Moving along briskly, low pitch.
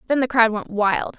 No: fast, 255 wpm; high, 230 Hz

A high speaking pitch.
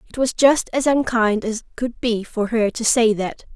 Yes: high, 230 Hz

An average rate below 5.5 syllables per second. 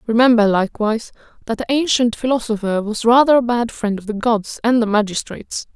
No: 5.9 syllables/s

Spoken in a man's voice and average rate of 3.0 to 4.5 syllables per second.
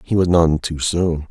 Yes: male; 4.1 syllables/s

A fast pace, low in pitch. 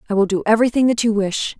No: fast, 265 wpm; high, 220 Hz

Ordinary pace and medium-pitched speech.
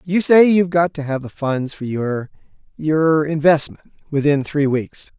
Yes: average, 160 wpm; medium, 150 Hz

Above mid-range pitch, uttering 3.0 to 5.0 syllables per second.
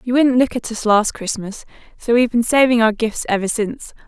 No: high, 230 Hz; 5.6 syllables/s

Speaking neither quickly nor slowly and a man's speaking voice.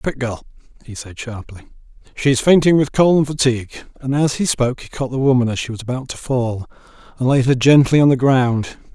No: fast, 220 wpm; male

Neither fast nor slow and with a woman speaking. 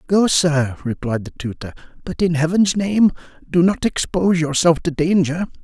No: average, 160 wpm; male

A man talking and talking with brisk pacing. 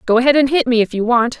No: female; fast, 345 wpm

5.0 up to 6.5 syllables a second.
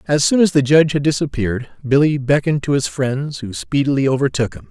Yes: 6.1 syllables/s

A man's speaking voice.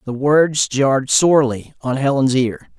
Yes: male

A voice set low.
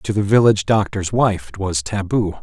Yes: low, 100 Hz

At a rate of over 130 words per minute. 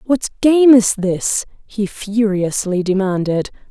No: slow, 115 wpm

